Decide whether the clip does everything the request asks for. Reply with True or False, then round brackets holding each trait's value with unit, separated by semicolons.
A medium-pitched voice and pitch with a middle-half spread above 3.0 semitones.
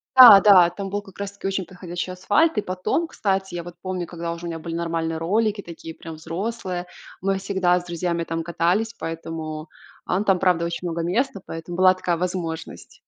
False (180 Hz; 2.6 semitones)